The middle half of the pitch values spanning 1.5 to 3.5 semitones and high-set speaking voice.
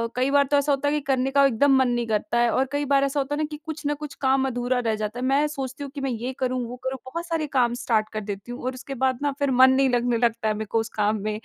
Yes: average, 2.9 semitones; very high, 260 Hz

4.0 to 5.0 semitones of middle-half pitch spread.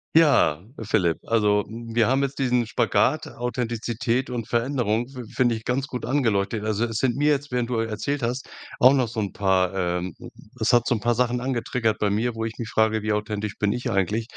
No: average, 2.7 semitones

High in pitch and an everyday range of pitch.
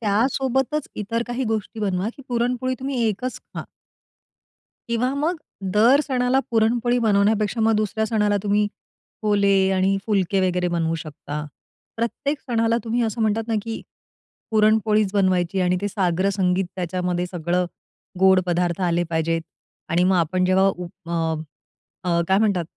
Yes: high, 205 Hz; average, 4.2 semitones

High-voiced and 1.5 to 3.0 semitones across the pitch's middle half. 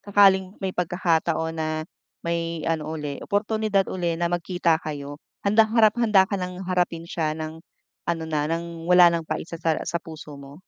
No: medium, 170 Hz; average, 2.7 semitones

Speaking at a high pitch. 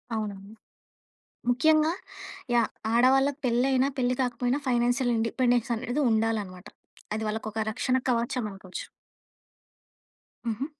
Yes: high, 240 Hz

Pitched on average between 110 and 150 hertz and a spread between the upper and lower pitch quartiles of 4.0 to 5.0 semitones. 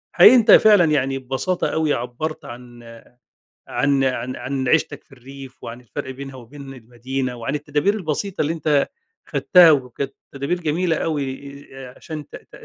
No: medium, 140 Hz; average, 3.2 semitones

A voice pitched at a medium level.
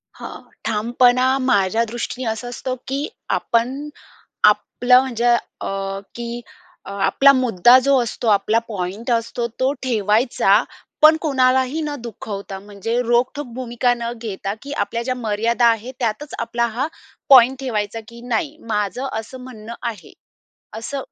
No: high, 235 Hz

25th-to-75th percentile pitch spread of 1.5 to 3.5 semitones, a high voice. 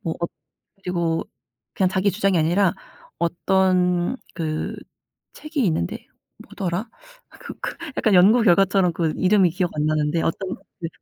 No: narrow, 2.6 semitones; medium, 180 Hz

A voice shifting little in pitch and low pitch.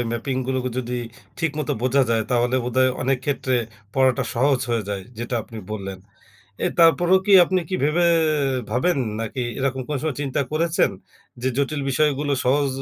No: average, 3.3 semitones; low, 130 Hz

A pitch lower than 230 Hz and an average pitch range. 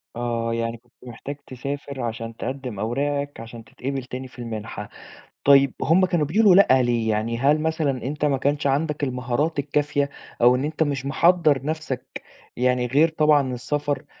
Yes: low, 135 Hz; average, 3.5 semitones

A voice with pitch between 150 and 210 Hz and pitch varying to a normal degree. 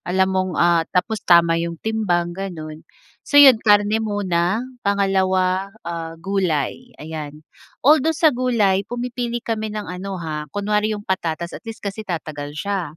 Yes: high, 190 Hz; average, 4.2 semitones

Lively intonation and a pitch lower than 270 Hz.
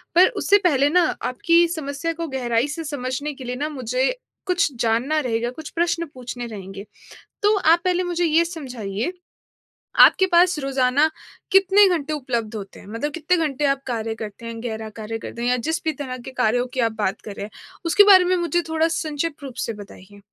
No: wide, 6.0 semitones; very high, 280 Hz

